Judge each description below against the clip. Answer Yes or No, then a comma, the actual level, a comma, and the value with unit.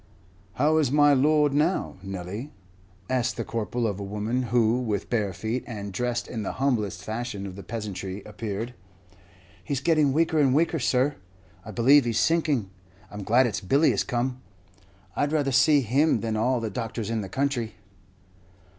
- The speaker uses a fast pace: No, average, 170 wpm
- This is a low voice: Yes, low, 120 Hz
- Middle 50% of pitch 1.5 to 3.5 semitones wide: No, average, 4.6 semitones